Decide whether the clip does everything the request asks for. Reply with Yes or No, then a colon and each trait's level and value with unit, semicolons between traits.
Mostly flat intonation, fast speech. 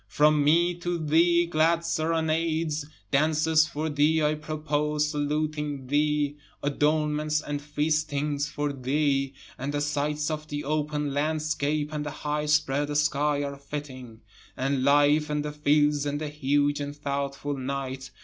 No: narrow, 1.1 semitones; average, 140 wpm